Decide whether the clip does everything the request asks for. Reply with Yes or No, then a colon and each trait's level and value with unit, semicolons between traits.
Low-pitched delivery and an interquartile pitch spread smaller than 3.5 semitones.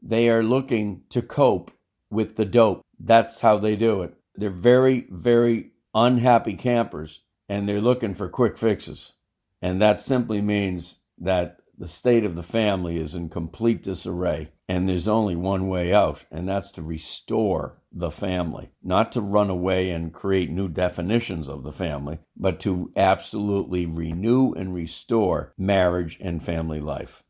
No: very low, 95 Hz; average, 4.5 semitones